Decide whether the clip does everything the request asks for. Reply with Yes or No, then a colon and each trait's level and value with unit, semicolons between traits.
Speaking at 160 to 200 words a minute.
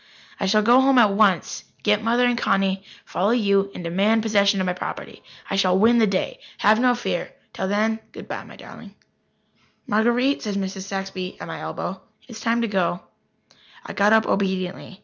Yes: average, 190 wpm